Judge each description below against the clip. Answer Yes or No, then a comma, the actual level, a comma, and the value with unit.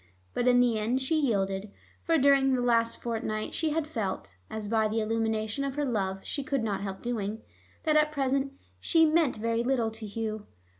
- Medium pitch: No, high, 230 Hz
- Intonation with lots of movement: No, average, 4.2 semitones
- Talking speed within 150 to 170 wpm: No, average, 195 wpm